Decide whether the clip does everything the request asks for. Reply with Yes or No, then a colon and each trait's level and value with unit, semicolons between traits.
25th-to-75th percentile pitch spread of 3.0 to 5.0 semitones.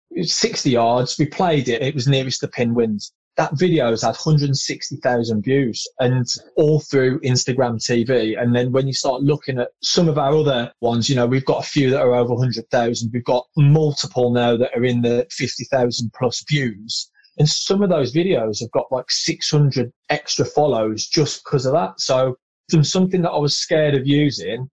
Yes: average, 3.6 semitones